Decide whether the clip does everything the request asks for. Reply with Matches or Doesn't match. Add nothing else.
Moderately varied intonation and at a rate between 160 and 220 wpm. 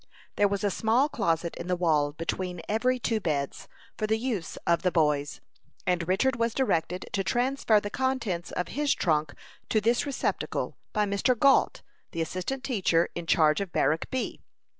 Doesn't match